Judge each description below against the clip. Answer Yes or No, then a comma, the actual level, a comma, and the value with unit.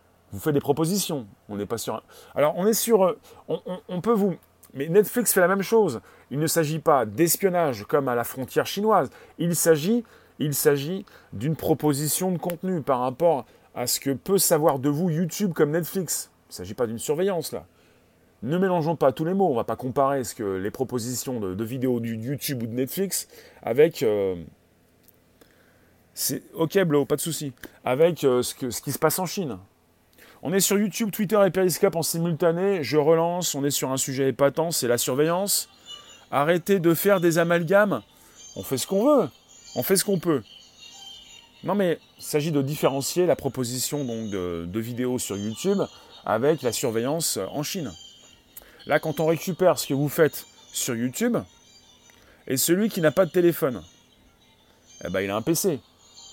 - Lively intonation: Yes, wide, 6.3 semitones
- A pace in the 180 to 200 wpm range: Yes, average, 190 wpm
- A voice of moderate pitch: Yes, medium, 150 Hz